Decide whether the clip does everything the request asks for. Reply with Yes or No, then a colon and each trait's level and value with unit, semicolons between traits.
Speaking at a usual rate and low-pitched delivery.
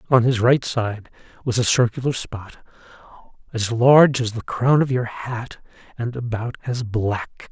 Yes: average, 160 wpm; low, 120 Hz